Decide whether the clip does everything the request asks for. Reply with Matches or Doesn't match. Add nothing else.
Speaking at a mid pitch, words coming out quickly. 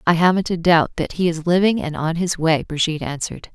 Matches